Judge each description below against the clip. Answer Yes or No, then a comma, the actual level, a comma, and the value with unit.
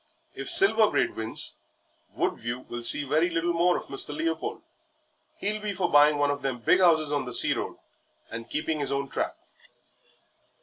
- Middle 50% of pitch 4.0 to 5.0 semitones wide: Yes, average, 4.7 semitones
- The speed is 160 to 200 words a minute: Yes, average, 175 wpm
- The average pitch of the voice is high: No, medium, 150 Hz